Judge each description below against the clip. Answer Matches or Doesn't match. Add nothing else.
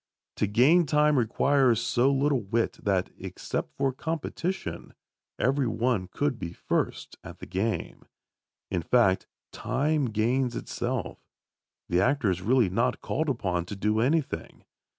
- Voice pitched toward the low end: Matches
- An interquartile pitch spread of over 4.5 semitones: Matches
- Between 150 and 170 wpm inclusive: Doesn't match